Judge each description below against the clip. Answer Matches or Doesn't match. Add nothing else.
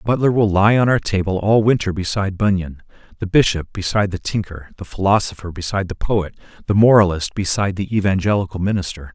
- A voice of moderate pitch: Doesn't match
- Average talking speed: Matches